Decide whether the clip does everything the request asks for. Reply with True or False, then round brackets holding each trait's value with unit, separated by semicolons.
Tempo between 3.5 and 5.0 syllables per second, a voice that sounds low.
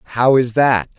True (4.8 syllables/s; 125 Hz)